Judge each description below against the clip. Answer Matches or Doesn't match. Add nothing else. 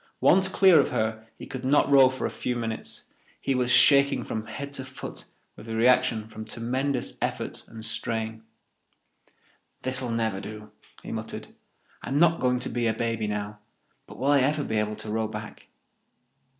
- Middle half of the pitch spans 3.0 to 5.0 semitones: Matches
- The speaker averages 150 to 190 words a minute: Matches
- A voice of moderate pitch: Doesn't match